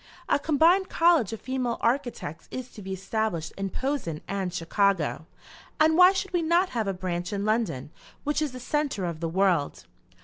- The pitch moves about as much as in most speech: No, wide, 8.3 semitones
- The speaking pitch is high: Yes, high, 220 Hz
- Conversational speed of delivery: Yes, average, 180 wpm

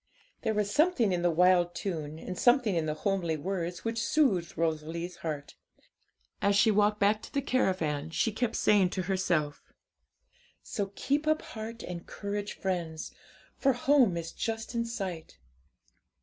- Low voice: No, high, 190 Hz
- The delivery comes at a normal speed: Yes, average, 155 wpm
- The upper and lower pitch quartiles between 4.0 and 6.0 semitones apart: Yes, average, 4.8 semitones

